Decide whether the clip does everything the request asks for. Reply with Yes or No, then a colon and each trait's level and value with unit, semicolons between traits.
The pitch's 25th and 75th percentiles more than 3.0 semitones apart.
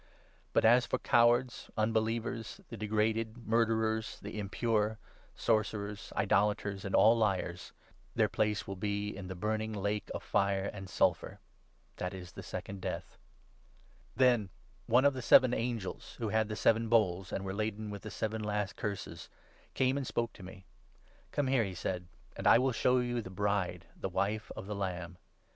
No: narrow, 2.6 semitones